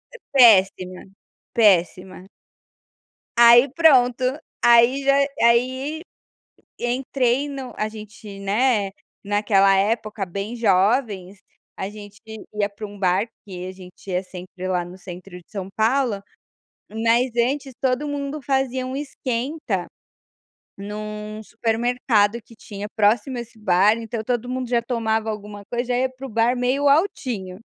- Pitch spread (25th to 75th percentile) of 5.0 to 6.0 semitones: No, average, 4.0 semitones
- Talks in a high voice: Yes, high, 225 Hz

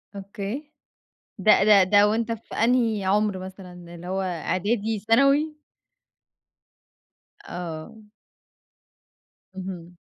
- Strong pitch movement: No, average, 3.4 semitones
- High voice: Yes, high, 205 Hz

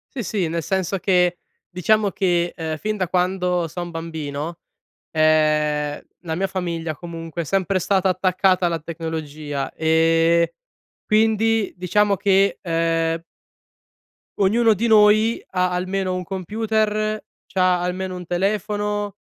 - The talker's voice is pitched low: No, medium, 180 Hz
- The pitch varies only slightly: No, average, 3.2 semitones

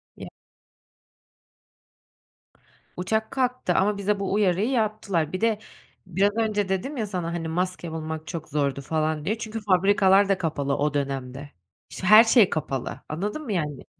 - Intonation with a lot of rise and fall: No, average, 5.0 semitones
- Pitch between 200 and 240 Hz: No, medium, 185 Hz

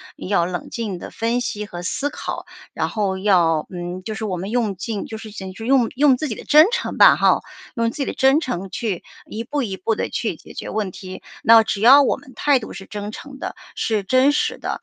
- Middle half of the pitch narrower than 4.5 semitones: No, average, 5.1 semitones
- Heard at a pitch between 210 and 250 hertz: Yes, high, 220 Hz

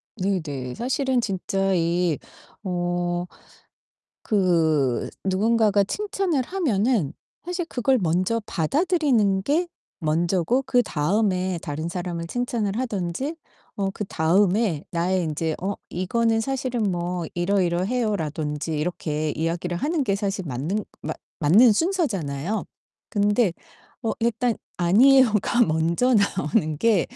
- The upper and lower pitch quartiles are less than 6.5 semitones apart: Yes, wide, 5.4 semitones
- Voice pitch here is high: Yes, high, 195 Hz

